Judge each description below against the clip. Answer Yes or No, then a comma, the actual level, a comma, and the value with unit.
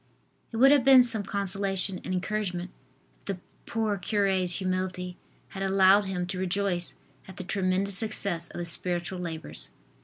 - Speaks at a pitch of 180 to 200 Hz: Yes, high, 190 Hz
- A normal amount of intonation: No, narrow, 1.8 semitones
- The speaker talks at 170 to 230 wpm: No, average, 155 wpm